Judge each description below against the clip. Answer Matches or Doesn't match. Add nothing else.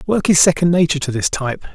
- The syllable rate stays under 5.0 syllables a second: Doesn't match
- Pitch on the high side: Doesn't match